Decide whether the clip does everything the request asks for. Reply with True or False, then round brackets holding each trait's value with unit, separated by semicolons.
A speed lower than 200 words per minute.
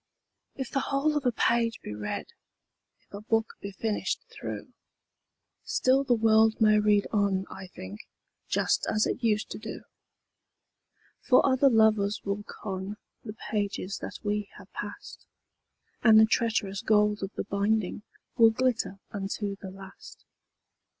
True (150 wpm)